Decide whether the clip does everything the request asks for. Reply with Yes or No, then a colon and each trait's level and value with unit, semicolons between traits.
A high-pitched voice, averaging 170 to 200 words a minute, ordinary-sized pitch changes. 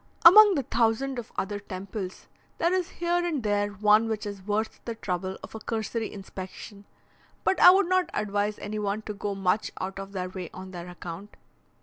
Yes: high, 210 Hz; average, 195 wpm; average, 3.1 semitones